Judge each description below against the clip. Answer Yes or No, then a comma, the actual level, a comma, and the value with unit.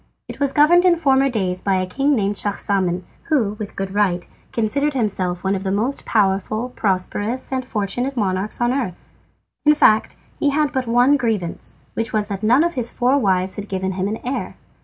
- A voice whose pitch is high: Yes, high, 215 Hz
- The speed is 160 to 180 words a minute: No, average, 200 wpm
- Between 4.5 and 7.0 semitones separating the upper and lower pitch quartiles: Yes, wide, 5.5 semitones